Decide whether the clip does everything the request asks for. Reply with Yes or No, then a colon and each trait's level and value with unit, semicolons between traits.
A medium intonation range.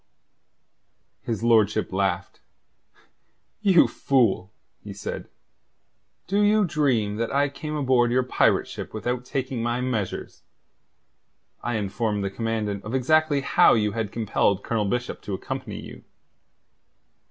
Yes: average, 4.2 semitones